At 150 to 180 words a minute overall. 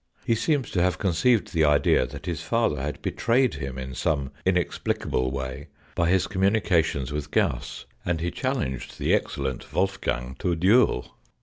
Yes: average, 170 wpm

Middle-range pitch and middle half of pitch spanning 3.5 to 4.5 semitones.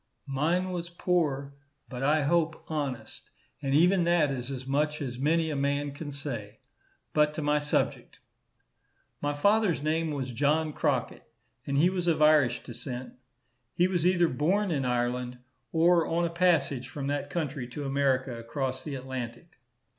Yes: medium, 145 Hz; average, 3.8 semitones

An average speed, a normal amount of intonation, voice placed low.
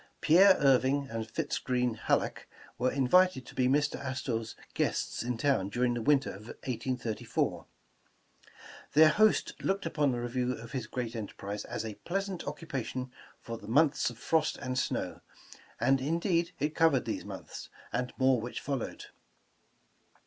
Yes: average, 155 wpm; average, 3.7 semitones; low, 130 Hz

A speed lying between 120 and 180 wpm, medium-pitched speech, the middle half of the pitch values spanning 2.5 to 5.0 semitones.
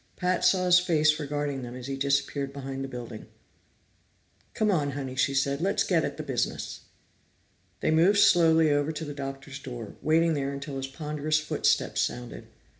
Yes: average, 175 wpm; medium, 145 Hz; average, 2.8 semitones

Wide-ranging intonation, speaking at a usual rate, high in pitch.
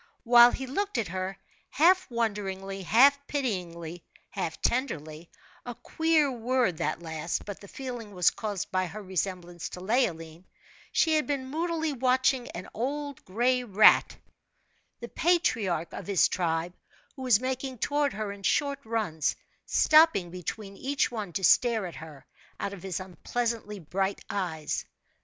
Yes: wide, 6.2 semitones; average, 145 wpm; high, 215 Hz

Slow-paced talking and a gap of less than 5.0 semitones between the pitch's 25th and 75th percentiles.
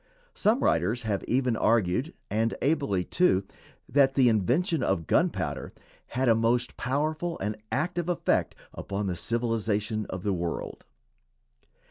No: slow, 130 wpm; wide, 5.5 semitones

